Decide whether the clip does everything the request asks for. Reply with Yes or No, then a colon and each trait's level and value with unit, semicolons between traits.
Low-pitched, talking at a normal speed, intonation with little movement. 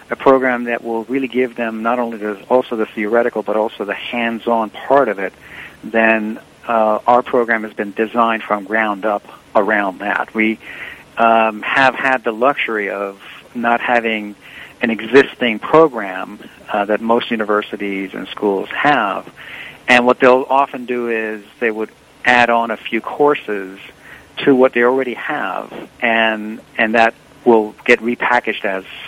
Yes: low, 115 Hz; average, 155 wpm; narrow, 2.0 semitones